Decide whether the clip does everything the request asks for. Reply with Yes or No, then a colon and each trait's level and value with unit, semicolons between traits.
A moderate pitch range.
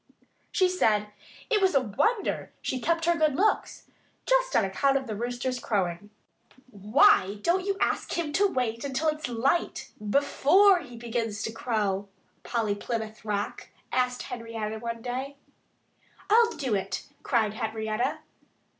No: wide, 6.1 semitones